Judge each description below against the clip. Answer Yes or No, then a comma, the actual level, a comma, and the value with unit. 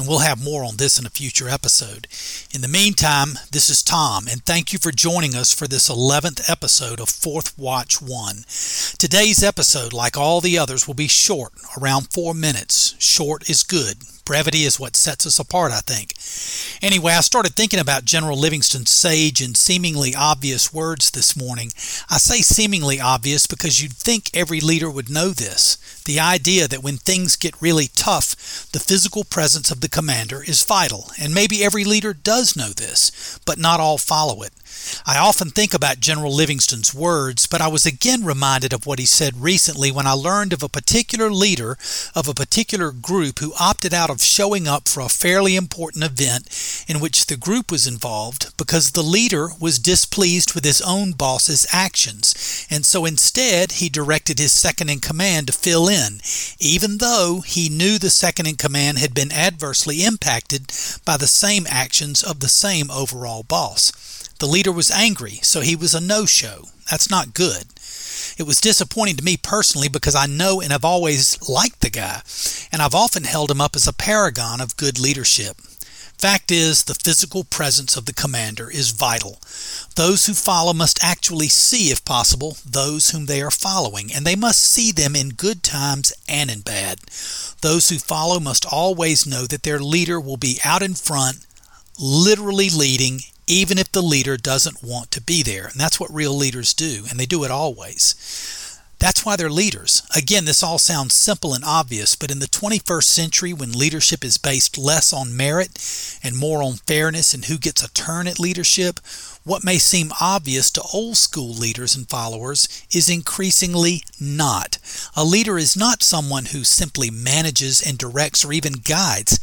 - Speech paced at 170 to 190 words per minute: Yes, average, 185 wpm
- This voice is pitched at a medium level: Yes, medium, 155 Hz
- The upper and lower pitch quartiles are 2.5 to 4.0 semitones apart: No, average, 4.6 semitones